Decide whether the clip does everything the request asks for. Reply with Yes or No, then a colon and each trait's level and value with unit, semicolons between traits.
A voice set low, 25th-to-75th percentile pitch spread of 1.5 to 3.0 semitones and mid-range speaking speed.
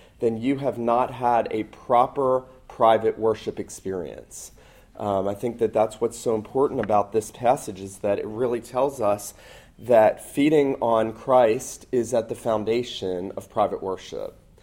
Yes: low, 115 Hz; average, 2.7 semitones; average, 155 wpm